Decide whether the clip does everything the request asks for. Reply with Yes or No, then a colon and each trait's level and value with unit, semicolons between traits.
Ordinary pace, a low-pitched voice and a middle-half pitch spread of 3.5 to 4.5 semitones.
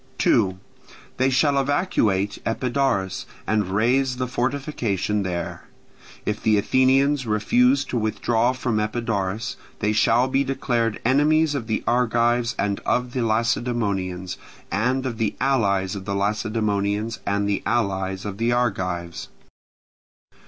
No: slow, 125 wpm; low, 115 Hz; average, 4.1 semitones